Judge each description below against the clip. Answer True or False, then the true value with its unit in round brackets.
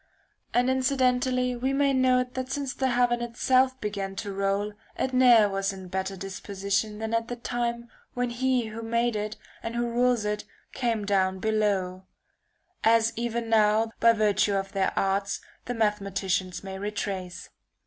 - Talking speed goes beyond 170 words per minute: False (160 wpm)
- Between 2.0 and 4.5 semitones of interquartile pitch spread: True (3.7 semitones)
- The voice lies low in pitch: False (225 Hz)